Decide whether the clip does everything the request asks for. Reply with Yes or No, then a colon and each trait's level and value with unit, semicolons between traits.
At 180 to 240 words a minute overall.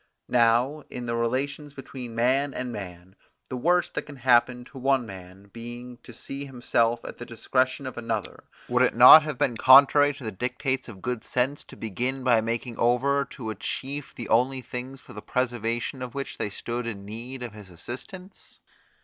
Yes: average, 190 wpm